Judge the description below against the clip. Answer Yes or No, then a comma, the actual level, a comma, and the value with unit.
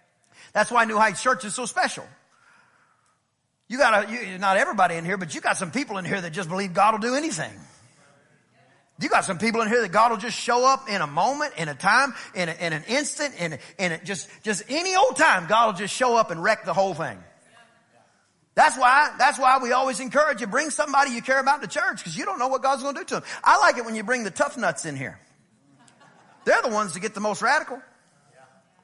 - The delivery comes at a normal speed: No, fast, 245 wpm